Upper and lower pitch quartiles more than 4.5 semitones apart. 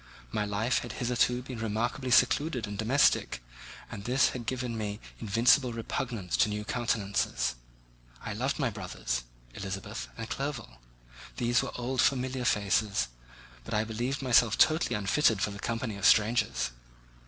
No: average, 3.3 semitones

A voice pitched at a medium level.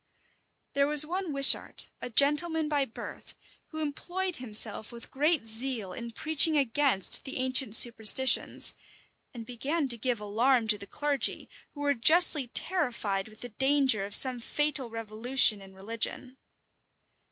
No: very high, 260 Hz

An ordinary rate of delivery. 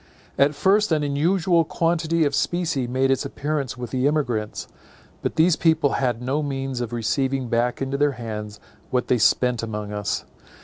Yes: average, 170 wpm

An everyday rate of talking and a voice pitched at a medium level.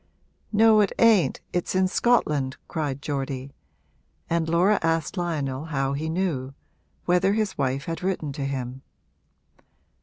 No: slow, 130 wpm; medium, 160 Hz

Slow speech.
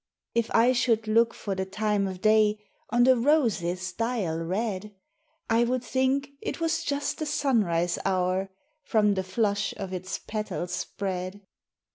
No: average, 150 wpm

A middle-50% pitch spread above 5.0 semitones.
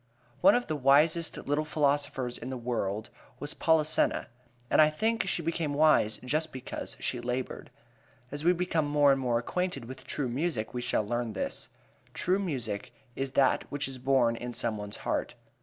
No: average, 4.2 semitones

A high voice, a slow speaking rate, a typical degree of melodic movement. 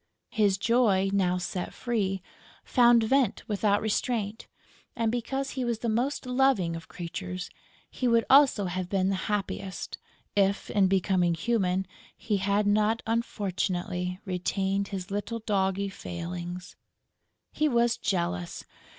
Yes: high, 200 Hz; slow, 130 wpm; average, 3.9 semitones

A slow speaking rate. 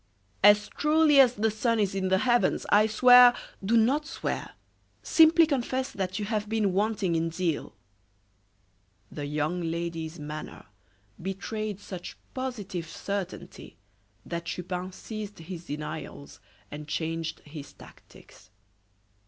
Yes: slow, 130 wpm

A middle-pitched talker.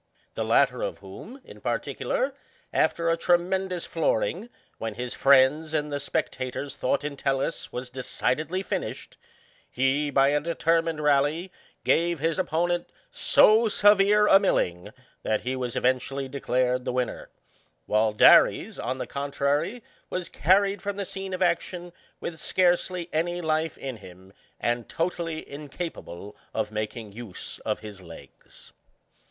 Yes: medium, 150 Hz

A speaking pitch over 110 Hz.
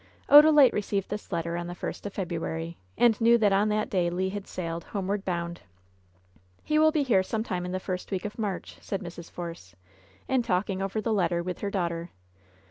Yes: high, 190 Hz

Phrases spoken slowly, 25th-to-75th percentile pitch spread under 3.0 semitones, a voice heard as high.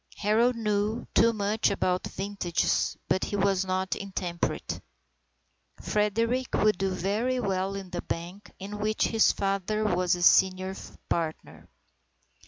Yes: slow, 130 wpm; narrow, 2.4 semitones; high, 195 Hz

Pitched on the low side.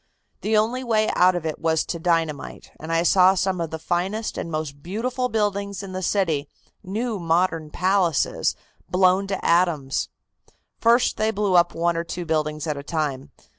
No: medium, 180 Hz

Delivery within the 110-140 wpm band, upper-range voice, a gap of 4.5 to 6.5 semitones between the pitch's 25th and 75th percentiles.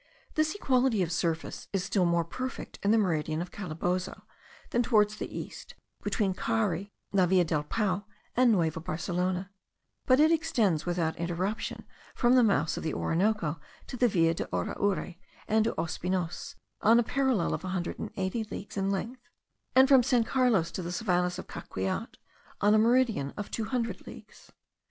No: average, 175 wpm; high, 195 Hz; average, 4.9 semitones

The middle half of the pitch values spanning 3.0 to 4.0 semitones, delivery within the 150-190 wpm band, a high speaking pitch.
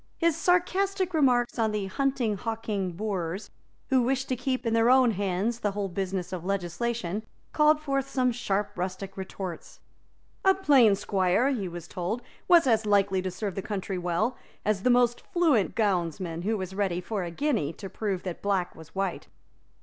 No: average, 5.1 semitones; average, 175 wpm; high, 210 Hz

